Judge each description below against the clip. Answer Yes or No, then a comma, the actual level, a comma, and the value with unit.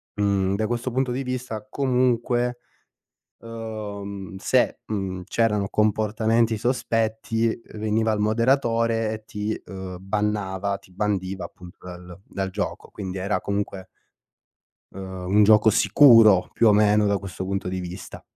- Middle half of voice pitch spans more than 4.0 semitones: No, average, 2.8 semitones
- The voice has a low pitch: Yes, low, 105 Hz